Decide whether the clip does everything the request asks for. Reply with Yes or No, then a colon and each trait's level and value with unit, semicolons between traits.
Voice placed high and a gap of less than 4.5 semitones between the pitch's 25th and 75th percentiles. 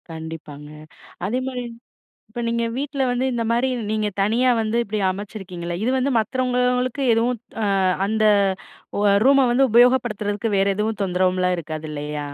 No: high, 220 Hz; average, 5.2 semitones